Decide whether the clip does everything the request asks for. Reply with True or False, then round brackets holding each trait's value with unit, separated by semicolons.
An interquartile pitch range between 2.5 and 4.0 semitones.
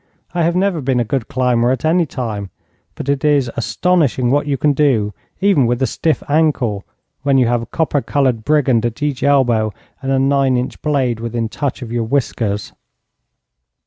True (3.6 semitones)